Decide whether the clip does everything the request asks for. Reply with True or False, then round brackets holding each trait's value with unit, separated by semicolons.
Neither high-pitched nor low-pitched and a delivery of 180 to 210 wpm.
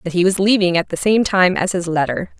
False (180 Hz; 275 wpm)